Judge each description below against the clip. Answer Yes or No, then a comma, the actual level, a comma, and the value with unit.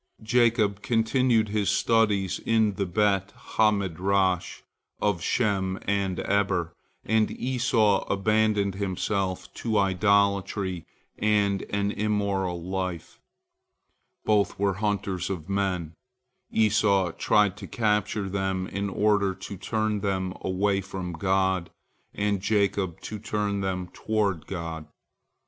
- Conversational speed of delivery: No, slow, 115 wpm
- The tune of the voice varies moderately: No, narrow, 2.0 semitones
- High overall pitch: No, low, 100 Hz